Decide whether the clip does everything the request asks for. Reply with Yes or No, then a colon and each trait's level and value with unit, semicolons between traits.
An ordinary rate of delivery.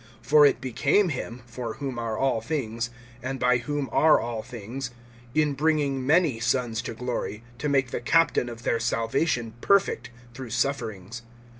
Yes: average, 160 wpm